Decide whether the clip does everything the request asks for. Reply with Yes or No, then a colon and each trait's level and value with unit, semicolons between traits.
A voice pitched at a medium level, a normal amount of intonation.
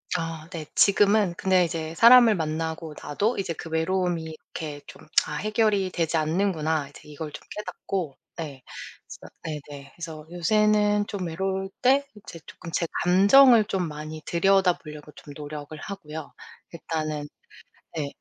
Yes: medium, 170 Hz; average, 4.1 semitones